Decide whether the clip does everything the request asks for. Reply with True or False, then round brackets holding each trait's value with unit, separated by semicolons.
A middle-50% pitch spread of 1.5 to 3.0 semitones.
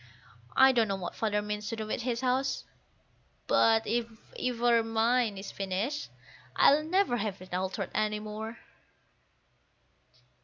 True (2.6 semitones)